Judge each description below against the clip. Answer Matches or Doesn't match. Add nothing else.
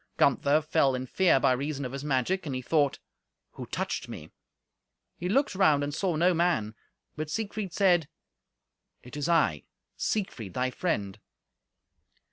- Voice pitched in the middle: Matches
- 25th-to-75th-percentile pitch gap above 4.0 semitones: Matches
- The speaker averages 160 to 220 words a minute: Doesn't match